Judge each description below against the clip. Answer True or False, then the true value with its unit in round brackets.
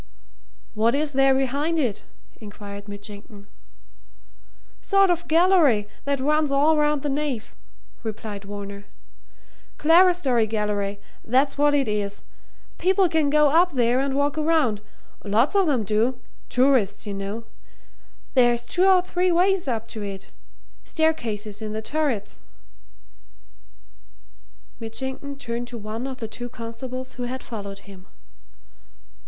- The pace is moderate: False (130 wpm)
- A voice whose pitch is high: True (255 Hz)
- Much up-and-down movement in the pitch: True (5.8 semitones)